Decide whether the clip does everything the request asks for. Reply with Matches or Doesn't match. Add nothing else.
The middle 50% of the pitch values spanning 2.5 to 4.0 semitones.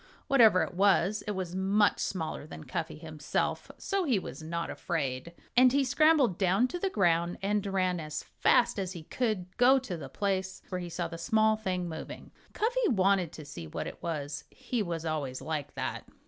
Doesn't match